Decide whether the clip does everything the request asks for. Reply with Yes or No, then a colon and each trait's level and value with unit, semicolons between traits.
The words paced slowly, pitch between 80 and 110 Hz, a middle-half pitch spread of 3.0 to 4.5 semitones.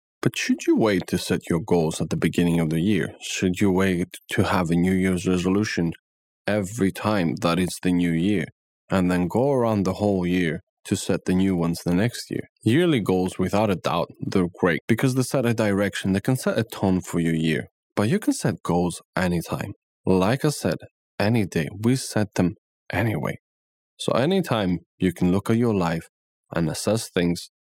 No: average, 200 wpm; very low, 95 Hz; average, 3.6 semitones